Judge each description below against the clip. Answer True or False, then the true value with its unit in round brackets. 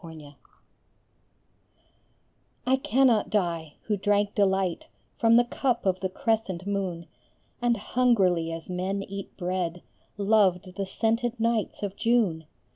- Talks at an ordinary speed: False (125 wpm)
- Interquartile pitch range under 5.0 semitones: True (3.9 semitones)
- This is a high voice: True (200 Hz)